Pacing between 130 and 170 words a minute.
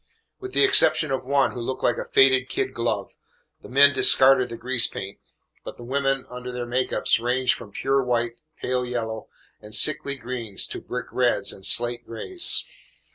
No: average, 185 wpm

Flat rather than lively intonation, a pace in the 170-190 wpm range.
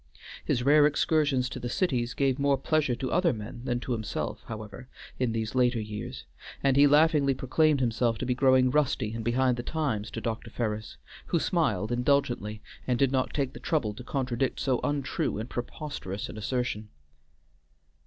No: average, 3.5 semitones; average, 175 wpm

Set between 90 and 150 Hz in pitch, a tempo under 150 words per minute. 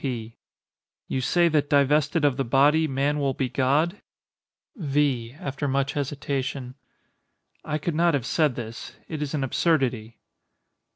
Yes: medium, 140 Hz; average, 140 wpm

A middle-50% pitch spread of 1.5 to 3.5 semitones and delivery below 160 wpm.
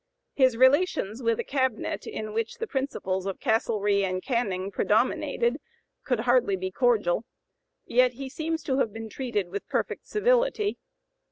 No: average, 4.4 semitones; average, 150 wpm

